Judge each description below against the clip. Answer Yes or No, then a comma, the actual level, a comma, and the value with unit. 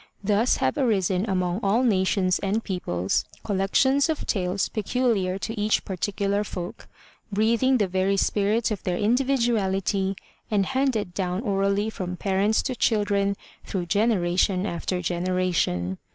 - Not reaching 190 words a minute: Yes, slow, 135 wpm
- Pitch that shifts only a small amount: No, average, 3.0 semitones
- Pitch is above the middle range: Yes, high, 200 Hz